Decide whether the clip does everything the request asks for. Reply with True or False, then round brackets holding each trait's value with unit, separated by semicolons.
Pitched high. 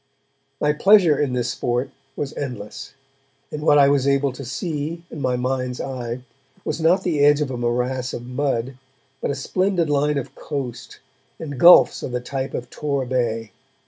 False (135 Hz)